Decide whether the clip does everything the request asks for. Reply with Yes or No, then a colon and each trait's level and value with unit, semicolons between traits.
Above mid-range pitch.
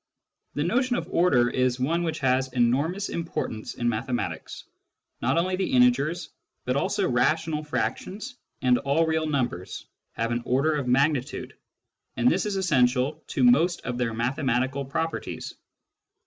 No: medium, 140 Hz